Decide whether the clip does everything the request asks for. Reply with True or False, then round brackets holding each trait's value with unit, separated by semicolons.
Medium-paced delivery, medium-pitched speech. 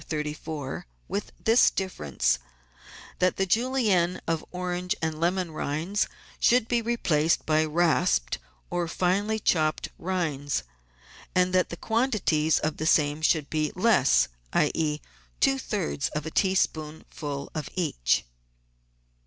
False (120 wpm; 170 Hz)